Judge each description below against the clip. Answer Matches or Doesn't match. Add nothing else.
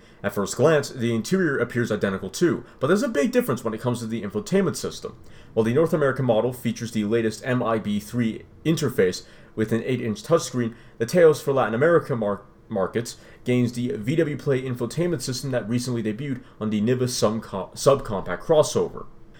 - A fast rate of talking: Doesn't match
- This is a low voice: Matches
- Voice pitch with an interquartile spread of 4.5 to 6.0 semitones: Doesn't match